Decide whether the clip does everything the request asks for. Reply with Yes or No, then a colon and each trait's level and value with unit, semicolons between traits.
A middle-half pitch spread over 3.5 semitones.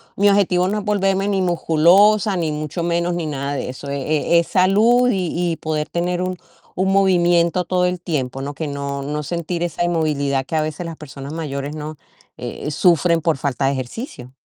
Yes: average, 3.9 semitones